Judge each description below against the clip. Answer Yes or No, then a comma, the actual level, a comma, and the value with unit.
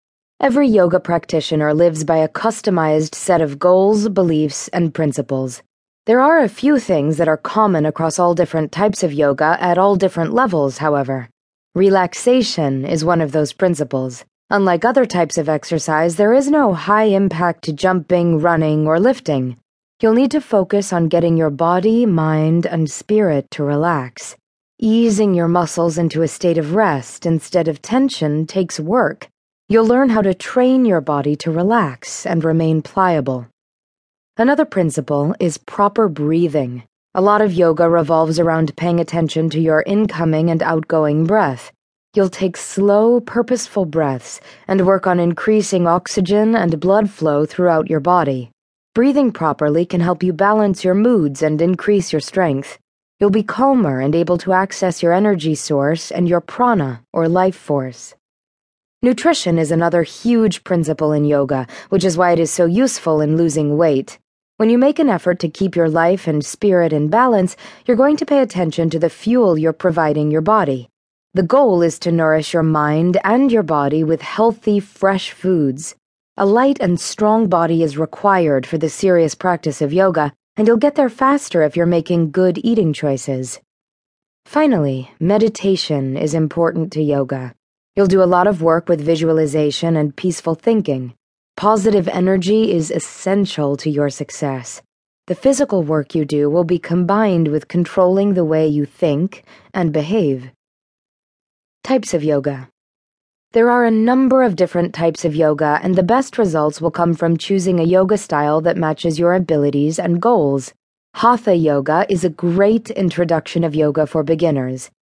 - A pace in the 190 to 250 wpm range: No, average, 165 wpm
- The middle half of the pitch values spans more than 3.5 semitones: Yes, average, 4.4 semitones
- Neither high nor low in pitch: Yes, medium, 170 Hz